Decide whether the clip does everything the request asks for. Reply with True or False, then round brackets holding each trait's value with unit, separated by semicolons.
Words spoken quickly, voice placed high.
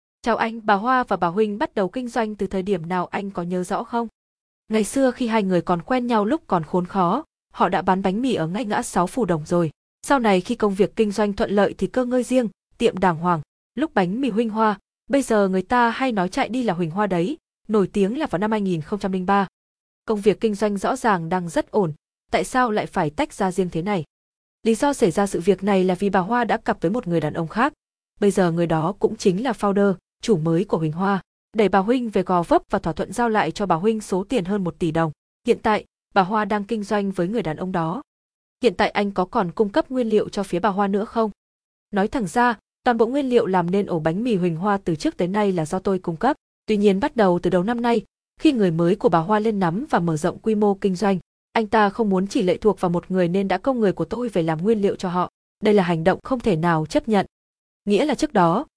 True (265 wpm; 205 Hz)